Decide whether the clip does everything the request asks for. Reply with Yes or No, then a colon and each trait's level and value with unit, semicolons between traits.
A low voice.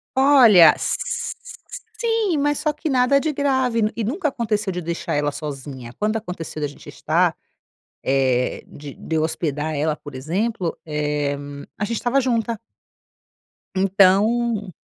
No: high, 205 Hz